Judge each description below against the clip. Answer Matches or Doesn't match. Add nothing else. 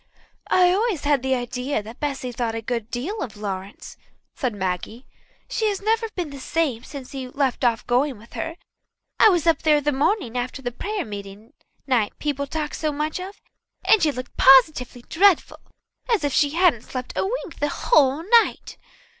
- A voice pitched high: Matches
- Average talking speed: Matches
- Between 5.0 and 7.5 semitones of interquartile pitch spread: Matches